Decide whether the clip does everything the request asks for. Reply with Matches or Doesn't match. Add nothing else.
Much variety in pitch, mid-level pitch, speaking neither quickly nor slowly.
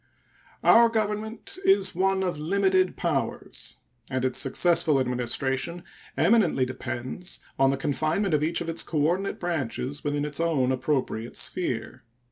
Doesn't match